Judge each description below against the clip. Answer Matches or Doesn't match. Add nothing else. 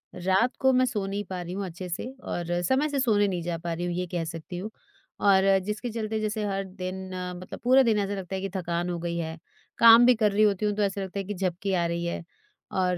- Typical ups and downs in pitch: Matches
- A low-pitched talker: Doesn't match